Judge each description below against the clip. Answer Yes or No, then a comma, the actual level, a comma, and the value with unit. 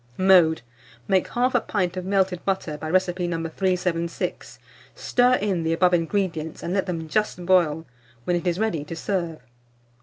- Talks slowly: No, average, 160 wpm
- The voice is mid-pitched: Yes, medium, 180 Hz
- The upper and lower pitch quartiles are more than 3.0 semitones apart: No, narrow, 2.6 semitones